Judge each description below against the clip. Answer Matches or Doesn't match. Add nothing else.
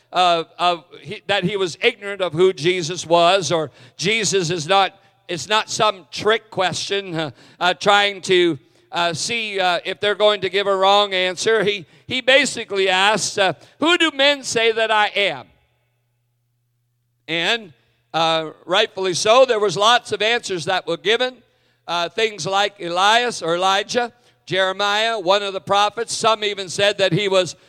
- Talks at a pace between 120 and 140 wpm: Doesn't match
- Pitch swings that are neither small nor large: Matches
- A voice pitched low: Doesn't match